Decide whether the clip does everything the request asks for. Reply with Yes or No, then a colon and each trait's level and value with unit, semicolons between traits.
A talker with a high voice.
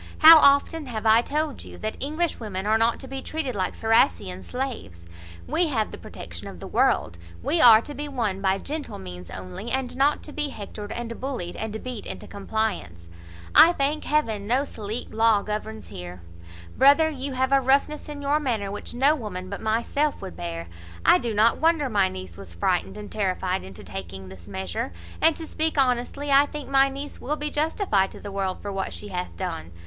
Yes: high, 225 Hz